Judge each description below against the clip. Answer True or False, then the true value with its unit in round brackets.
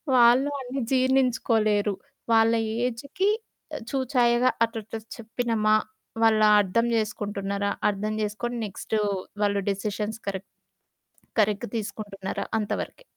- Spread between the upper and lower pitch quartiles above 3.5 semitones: False (2.9 semitones)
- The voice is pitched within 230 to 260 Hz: False (220 Hz)